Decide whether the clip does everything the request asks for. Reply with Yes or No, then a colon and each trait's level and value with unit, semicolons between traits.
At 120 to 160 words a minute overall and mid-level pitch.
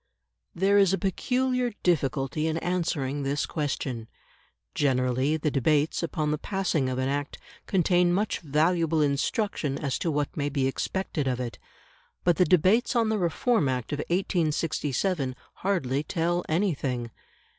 Yes: average, 145 wpm; medium, 155 Hz